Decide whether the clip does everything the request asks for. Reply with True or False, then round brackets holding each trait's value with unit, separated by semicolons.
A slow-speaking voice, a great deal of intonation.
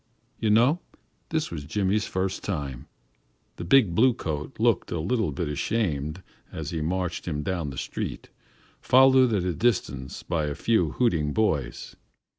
False (155 wpm; 6.7 semitones)